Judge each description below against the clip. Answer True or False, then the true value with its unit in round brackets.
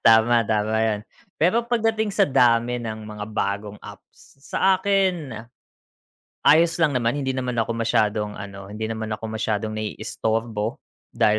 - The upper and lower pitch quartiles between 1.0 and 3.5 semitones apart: False (4.3 semitones)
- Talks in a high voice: False (115 Hz)